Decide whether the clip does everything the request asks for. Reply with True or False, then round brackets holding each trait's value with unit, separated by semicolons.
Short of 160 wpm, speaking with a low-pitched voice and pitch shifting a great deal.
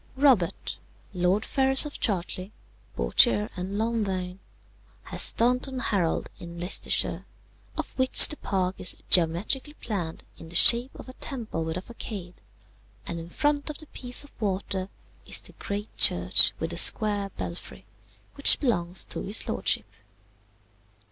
False (140 wpm; 195 Hz; 6.1 semitones)